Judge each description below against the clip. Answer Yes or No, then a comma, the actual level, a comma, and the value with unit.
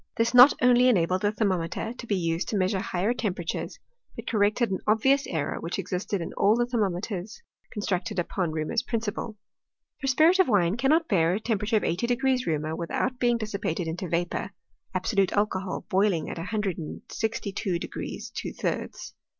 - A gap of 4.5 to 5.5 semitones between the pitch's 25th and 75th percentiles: Yes, average, 4.8 semitones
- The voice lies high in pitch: Yes, high, 205 Hz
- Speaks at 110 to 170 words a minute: No, average, 185 wpm